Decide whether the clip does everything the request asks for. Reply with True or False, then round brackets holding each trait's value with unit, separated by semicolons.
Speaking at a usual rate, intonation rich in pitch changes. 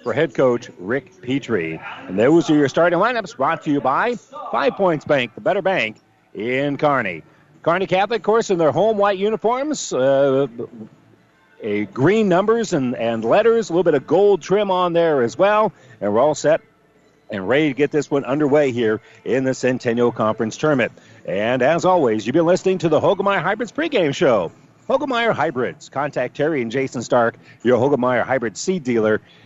True (185 wpm; 7.3 semitones)